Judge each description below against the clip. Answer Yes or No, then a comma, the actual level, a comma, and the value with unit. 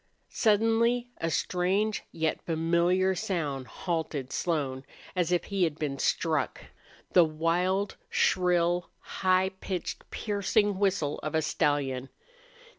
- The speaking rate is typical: No, slow, 115 wpm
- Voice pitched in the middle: Yes, medium, 175 Hz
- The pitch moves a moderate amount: Yes, average, 3.5 semitones